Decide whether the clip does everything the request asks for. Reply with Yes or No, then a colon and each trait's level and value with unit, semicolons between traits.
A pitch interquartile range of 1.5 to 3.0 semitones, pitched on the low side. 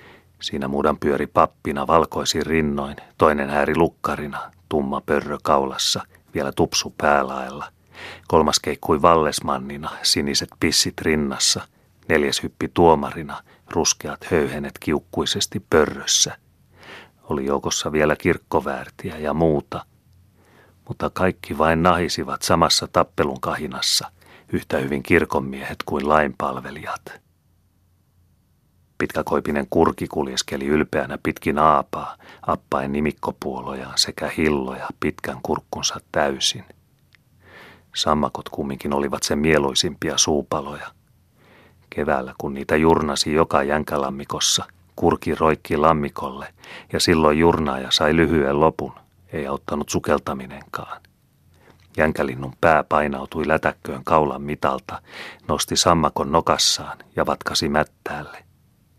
Yes: narrow, 2.6 semitones; very low, 75 Hz